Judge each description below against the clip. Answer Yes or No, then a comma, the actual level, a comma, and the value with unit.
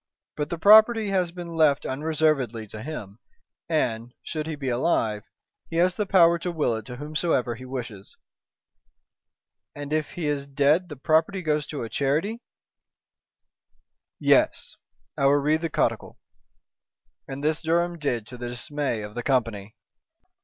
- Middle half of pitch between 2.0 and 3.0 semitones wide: No, average, 5.1 semitones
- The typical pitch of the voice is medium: Yes, medium, 150 Hz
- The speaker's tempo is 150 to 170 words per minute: Yes, average, 155 wpm